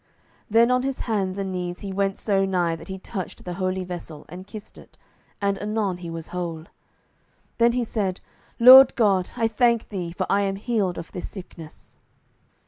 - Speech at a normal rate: Yes, average, 185 wpm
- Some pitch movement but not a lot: Yes, average, 3.4 semitones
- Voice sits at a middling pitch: No, high, 195 Hz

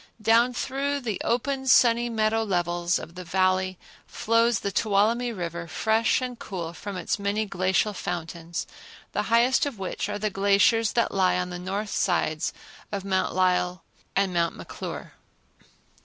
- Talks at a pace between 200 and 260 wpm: No, average, 155 wpm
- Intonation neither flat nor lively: Yes, average, 4.1 semitones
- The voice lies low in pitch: No, high, 200 Hz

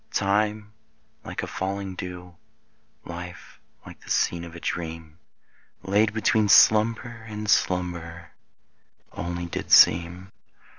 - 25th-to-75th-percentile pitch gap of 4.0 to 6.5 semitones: No, average, 3.4 semitones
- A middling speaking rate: No, slow, 110 wpm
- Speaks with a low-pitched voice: Yes, very low, 90 Hz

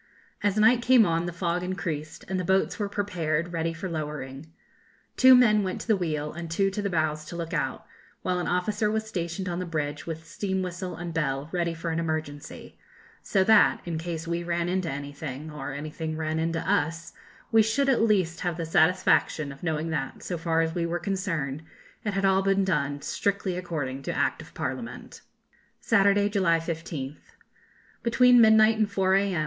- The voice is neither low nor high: Yes, medium, 170 Hz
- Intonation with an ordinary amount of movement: Yes, average, 3.6 semitones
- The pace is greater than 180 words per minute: Yes, average, 190 wpm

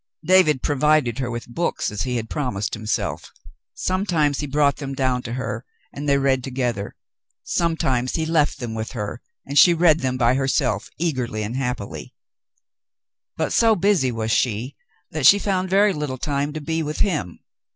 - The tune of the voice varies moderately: Yes, average, 4.4 semitones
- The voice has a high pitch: No, low, 135 Hz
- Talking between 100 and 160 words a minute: No, average, 170 wpm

